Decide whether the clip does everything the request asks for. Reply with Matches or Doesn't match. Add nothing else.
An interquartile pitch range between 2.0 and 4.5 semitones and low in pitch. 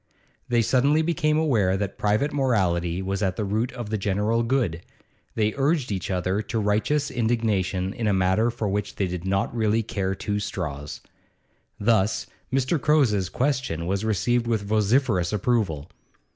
Matches